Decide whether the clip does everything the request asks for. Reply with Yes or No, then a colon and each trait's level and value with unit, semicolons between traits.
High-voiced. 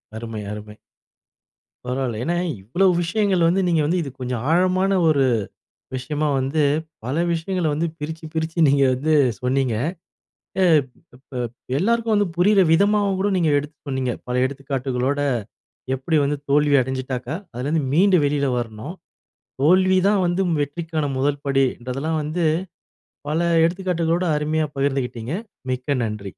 No: medium, 150 Hz